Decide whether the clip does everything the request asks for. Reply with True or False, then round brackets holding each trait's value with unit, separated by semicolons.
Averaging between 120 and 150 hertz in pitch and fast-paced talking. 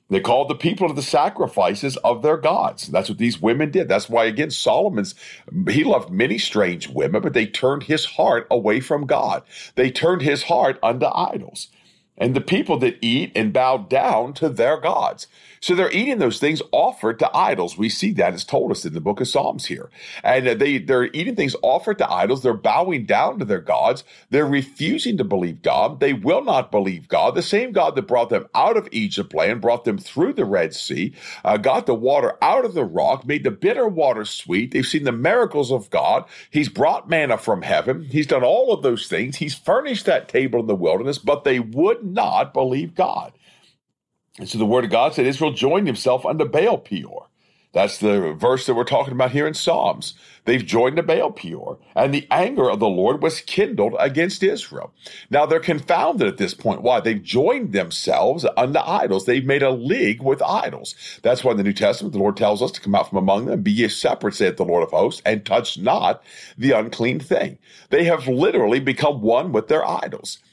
True (140 Hz; 210 wpm)